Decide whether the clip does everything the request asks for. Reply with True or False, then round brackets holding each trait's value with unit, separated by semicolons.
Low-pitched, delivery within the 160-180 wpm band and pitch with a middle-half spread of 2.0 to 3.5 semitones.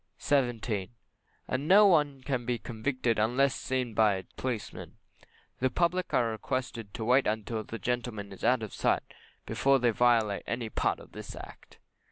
True (120 Hz; 170 wpm; 2.8 semitones)